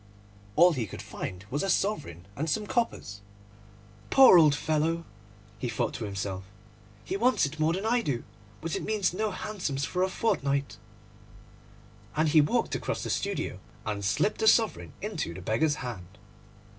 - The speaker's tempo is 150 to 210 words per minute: Yes, average, 165 wpm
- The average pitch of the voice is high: No, medium, 155 Hz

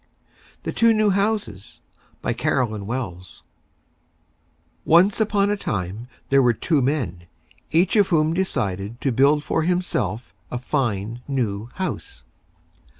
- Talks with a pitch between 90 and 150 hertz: Yes, low, 135 Hz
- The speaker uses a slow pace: Yes, slow, 125 wpm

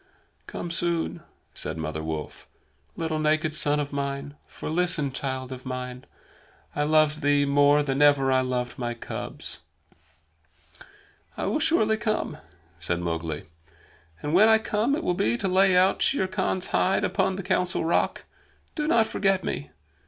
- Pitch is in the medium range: Yes, medium, 150 Hz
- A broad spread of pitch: Yes, wide, 6.3 semitones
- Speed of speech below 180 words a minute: Yes, average, 155 wpm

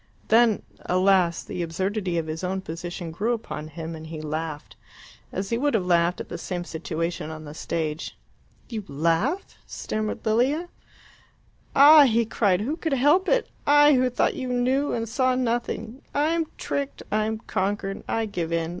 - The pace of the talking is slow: No, average, 170 wpm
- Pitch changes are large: Yes, wide, 7.0 semitones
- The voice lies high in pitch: Yes, high, 205 Hz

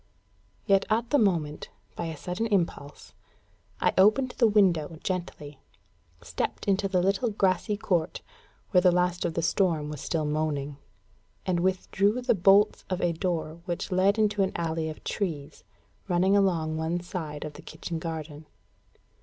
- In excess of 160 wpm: No, average, 155 wpm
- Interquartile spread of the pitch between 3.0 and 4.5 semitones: Yes, average, 3.6 semitones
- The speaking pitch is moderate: Yes, medium, 175 Hz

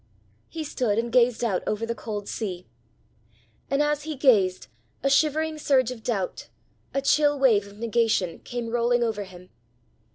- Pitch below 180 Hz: No, high, 235 Hz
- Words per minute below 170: Yes, average, 160 wpm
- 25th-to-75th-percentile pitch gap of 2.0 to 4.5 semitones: No, average, 4.9 semitones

